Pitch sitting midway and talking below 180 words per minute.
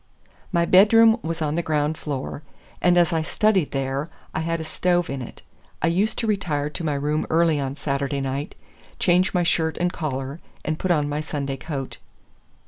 No: medium, 155 Hz; average, 190 wpm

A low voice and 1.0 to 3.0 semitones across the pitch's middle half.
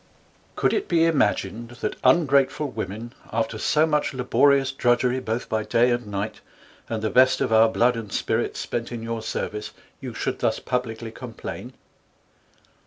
Yes: low, 120 Hz; average, 2.7 semitones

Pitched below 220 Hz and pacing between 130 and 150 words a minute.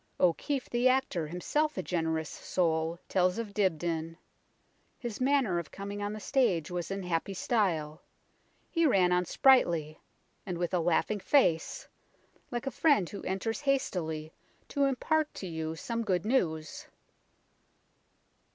Yes: medium, 185 Hz; average, 140 wpm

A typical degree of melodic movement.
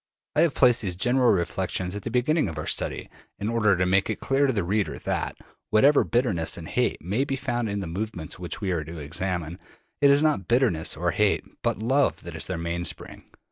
No: wide, 6.1 semitones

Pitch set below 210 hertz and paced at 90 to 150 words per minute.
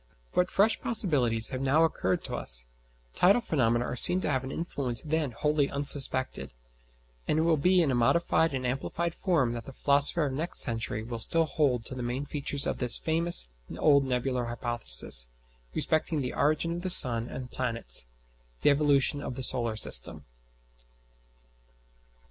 No: low, 135 Hz; average, 165 wpm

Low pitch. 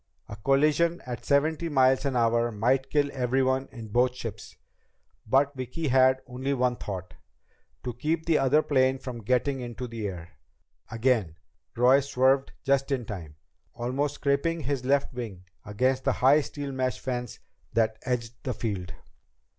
Yes: low, 130 Hz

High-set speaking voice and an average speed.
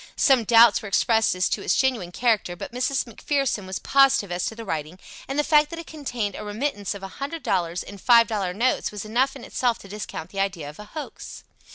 No: high, 225 Hz; fast, 230 wpm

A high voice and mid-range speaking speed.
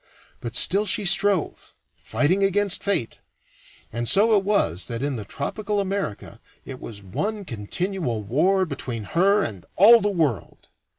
No: medium, 180 Hz; average, 150 wpm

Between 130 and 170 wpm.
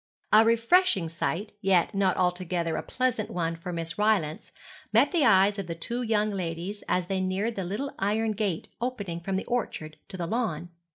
No: average, 185 wpm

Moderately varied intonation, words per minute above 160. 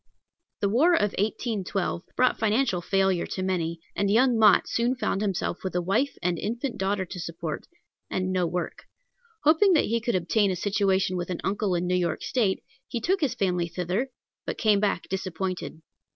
Yes: average, 4.1 semitones; average, 180 wpm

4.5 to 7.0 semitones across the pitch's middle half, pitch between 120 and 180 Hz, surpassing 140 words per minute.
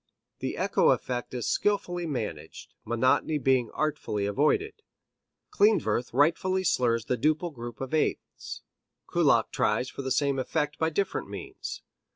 No: average, 5.3 semitones; medium, 140 Hz; slow, 135 wpm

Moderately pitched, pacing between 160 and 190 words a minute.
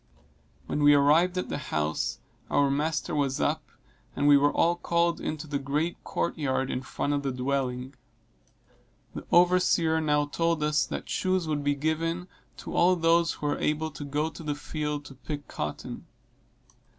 Yes: medium, 150 Hz; average, 175 wpm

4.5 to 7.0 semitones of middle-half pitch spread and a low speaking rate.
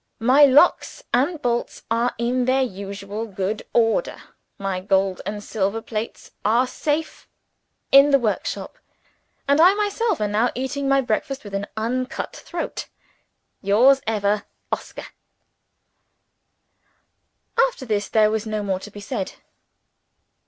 Yes: average, 4.9 semitones; slow, 130 wpm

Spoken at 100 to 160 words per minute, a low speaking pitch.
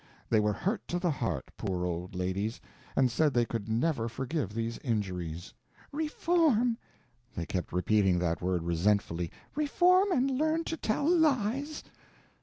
Yes: average, 145 wpm; low, 115 Hz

